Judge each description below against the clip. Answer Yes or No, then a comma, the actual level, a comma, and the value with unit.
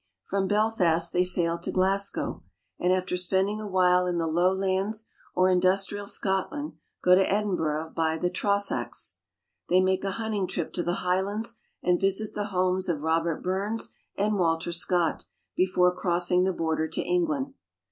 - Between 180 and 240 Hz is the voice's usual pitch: Yes, medium, 185 Hz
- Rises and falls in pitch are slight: Yes, narrow, 2.2 semitones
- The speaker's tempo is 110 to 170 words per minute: Yes, average, 155 wpm